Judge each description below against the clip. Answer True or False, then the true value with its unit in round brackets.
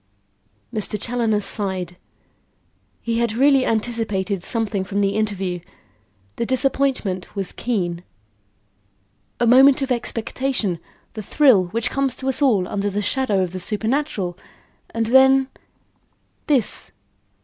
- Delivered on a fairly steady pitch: False (4.8 semitones)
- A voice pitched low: False (220 Hz)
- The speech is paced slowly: True (120 wpm)